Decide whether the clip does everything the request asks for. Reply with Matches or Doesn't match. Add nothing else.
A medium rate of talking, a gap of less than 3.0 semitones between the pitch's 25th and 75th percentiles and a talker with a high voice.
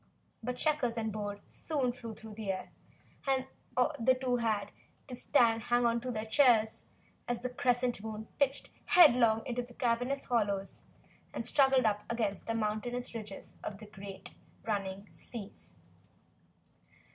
Matches